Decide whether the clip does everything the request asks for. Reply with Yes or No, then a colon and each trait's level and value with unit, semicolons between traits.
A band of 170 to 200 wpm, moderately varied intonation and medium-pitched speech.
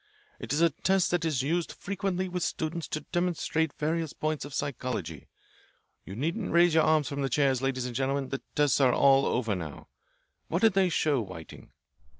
Yes: average, 185 wpm; average, 4.2 semitones; medium, 150 Hz